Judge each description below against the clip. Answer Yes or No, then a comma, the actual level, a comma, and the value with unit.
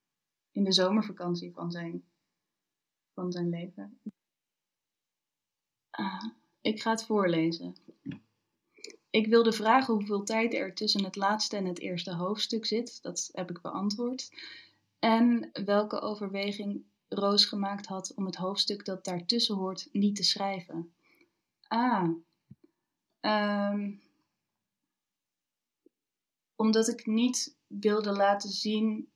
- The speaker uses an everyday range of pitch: Yes, average, 3.0 semitones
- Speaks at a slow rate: Yes, slow, 110 wpm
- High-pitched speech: Yes, high, 205 Hz